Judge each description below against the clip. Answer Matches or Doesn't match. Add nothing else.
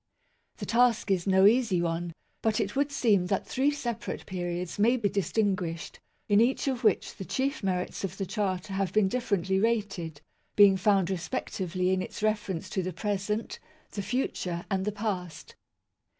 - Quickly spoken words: Doesn't match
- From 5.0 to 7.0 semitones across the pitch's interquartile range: Doesn't match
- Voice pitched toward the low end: Doesn't match